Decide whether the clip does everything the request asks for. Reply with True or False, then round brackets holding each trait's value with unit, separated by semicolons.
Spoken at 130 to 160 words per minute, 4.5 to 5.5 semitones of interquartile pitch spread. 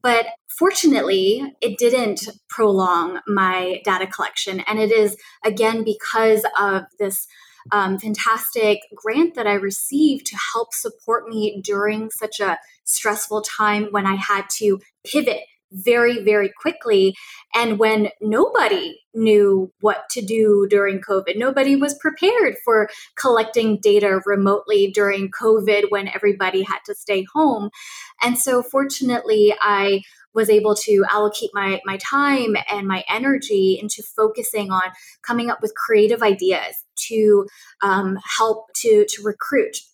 False (135 wpm; 3.1 semitones)